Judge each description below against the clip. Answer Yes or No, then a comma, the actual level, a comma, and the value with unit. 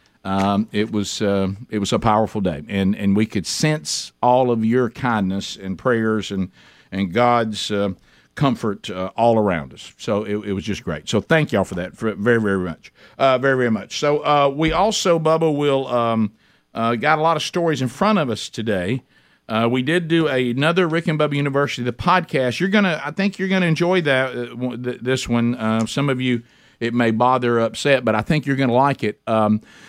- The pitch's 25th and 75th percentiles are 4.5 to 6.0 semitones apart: Yes, wide, 5.5 semitones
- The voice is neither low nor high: No, low, 120 Hz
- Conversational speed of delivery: No, fast, 210 wpm